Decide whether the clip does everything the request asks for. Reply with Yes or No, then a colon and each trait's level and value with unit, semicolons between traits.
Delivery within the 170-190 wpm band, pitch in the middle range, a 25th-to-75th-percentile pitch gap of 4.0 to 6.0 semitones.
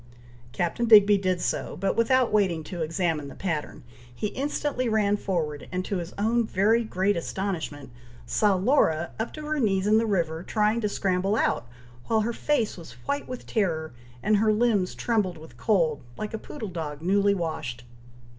No: average, 175 wpm; high, 200 Hz; average, 4.6 semitones